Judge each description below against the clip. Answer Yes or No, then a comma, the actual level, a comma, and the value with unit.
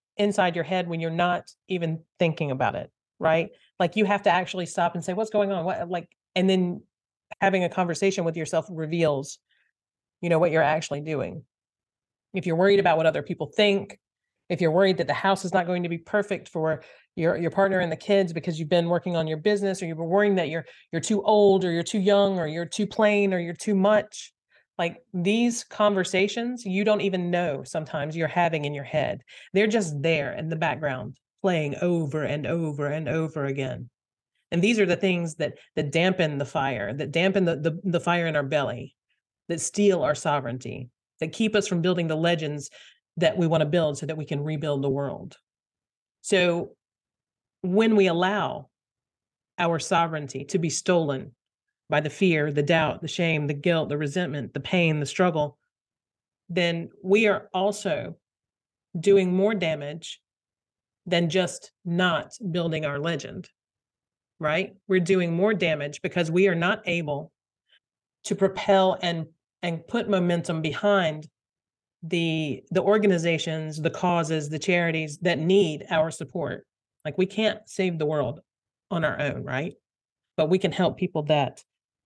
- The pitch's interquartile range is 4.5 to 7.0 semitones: No, average, 3.6 semitones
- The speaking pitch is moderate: Yes, medium, 170 Hz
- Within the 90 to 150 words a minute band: No, average, 175 wpm